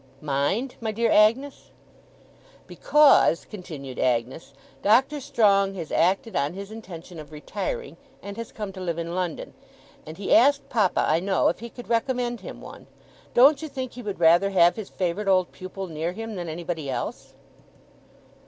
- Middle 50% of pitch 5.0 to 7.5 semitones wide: Yes, wide, 5.4 semitones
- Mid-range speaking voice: No, high, 195 Hz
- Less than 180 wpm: Yes, average, 165 wpm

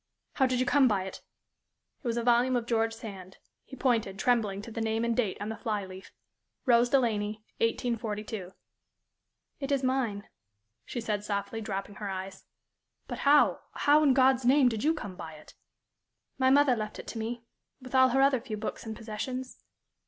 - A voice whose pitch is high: Yes, high, 230 Hz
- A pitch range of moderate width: Yes, average, 3.7 semitones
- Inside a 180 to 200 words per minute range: Yes, average, 185 wpm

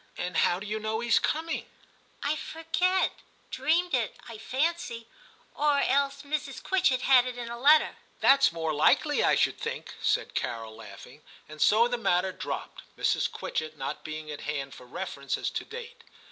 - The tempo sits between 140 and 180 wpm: No, average, 190 wpm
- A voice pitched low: No, high, 235 Hz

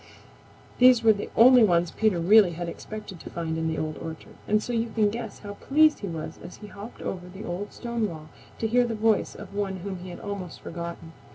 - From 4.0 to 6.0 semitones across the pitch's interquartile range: Yes, average, 4.4 semitones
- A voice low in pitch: No, high, 200 Hz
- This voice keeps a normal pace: No, fast, 225 wpm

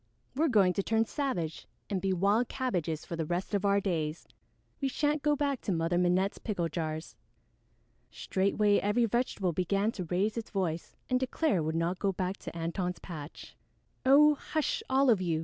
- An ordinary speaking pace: Yes, average, 185 wpm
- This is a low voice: No, high, 195 Hz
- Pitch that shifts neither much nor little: No, wide, 5.8 semitones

